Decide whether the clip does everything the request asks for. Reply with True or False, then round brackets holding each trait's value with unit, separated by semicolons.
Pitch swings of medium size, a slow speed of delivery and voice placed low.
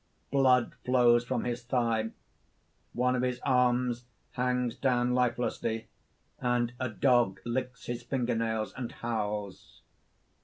False (1.5 semitones; 120 wpm; 120 Hz)